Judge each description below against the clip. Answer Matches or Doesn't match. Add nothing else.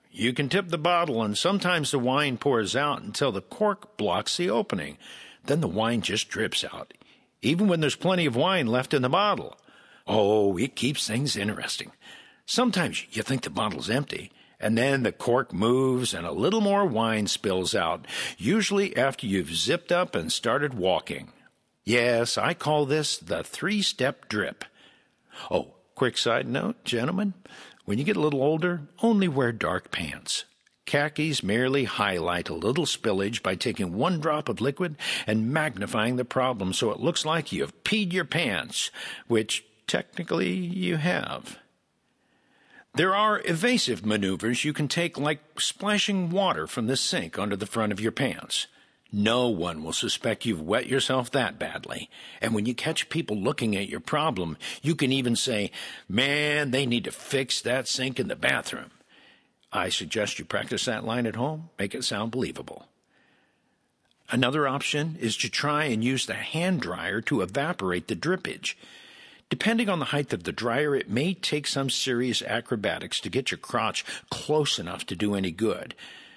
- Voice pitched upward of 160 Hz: Doesn't match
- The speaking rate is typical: Matches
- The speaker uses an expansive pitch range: Matches